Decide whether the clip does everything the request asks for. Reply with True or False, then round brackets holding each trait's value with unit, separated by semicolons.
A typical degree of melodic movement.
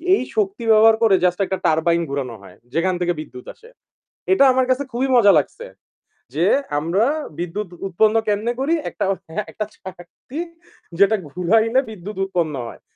True (4.7 semitones)